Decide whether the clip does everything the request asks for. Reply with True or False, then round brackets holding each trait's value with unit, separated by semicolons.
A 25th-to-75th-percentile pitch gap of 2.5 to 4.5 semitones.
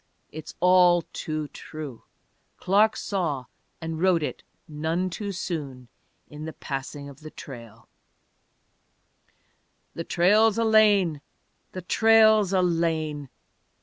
True (4.0 semitones)